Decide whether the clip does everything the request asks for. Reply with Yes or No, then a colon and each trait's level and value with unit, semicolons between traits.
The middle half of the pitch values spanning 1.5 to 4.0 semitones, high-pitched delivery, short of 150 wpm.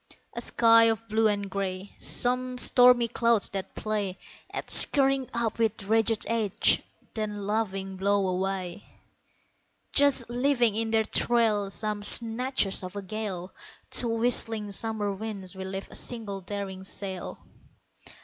Yes: average, 2.9 semitones; high, 215 Hz; slow, 135 wpm